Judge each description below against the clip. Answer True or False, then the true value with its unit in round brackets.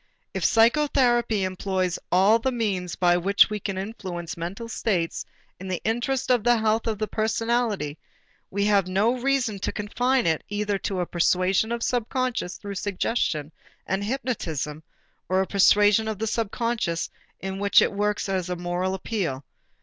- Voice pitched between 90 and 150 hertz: False (205 Hz)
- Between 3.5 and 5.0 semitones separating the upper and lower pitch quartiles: True (3.8 semitones)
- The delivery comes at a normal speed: True (165 wpm)